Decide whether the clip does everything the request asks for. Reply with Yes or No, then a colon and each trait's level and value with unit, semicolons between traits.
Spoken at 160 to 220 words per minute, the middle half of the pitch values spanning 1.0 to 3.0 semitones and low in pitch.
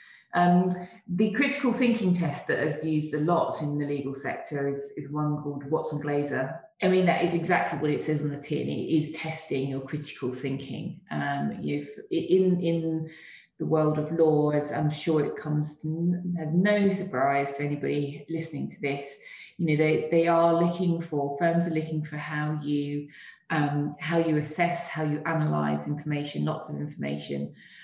No: average, 175 wpm; narrow, 2.6 semitones; medium, 150 Hz